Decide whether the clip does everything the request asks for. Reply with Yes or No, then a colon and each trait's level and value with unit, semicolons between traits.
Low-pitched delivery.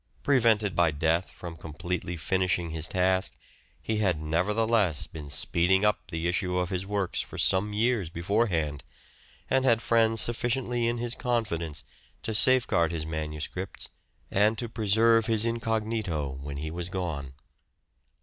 Yes: very low, 95 Hz